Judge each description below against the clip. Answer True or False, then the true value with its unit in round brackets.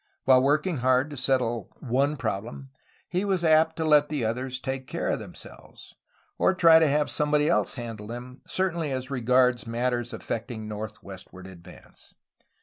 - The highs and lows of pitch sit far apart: False (4.2 semitones)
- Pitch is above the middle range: False (130 Hz)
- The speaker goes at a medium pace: True (160 wpm)